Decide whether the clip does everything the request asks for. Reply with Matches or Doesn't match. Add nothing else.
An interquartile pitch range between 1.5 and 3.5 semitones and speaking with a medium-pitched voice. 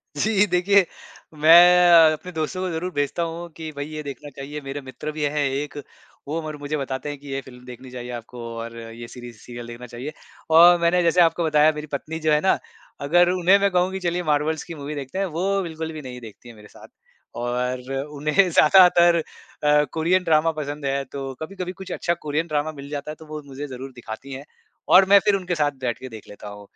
Doesn't match